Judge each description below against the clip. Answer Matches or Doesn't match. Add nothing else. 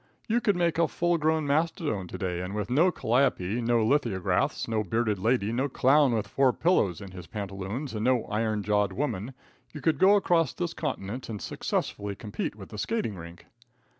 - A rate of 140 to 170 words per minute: Doesn't match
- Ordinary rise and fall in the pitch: Doesn't match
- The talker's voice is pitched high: Doesn't match